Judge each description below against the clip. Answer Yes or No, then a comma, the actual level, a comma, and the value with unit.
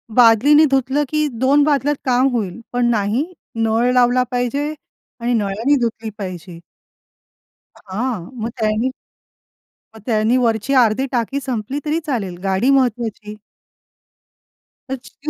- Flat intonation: No, average, 3.5 semitones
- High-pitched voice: Yes, high, 240 Hz